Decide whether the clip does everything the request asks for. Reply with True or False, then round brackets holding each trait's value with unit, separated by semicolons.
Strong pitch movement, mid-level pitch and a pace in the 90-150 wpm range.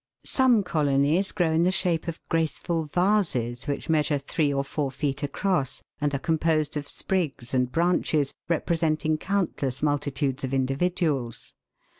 False (3.7 semitones; 155 Hz; 140 wpm)